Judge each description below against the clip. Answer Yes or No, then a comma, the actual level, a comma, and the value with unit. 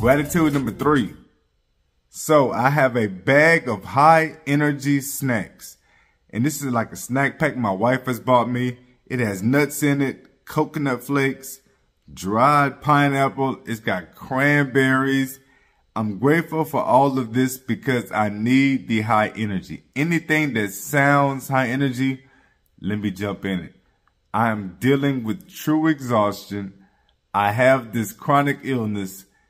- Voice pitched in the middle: No, low, 130 Hz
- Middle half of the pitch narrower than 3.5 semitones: No, average, 4.4 semitones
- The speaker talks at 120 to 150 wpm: Yes, average, 140 wpm